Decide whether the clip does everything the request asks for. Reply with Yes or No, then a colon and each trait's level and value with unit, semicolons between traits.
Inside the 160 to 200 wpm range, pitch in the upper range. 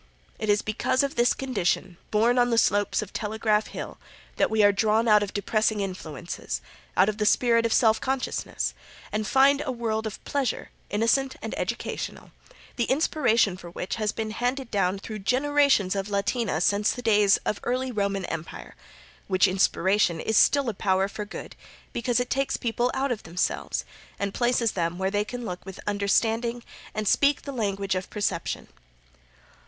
Yes: average, 175 wpm; high, 215 Hz